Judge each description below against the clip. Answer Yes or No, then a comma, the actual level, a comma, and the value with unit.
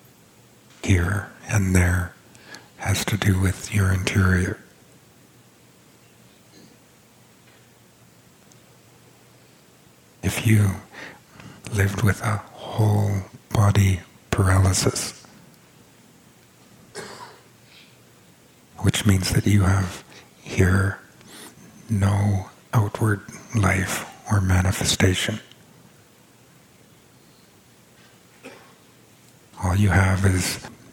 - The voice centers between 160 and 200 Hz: No, low, 100 Hz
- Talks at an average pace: No, slow, 60 wpm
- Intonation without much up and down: Yes, narrow, 1.9 semitones